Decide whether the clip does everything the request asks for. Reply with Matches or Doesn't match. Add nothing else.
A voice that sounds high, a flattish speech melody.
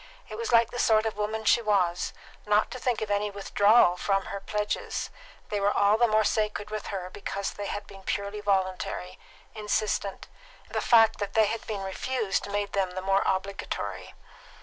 Matches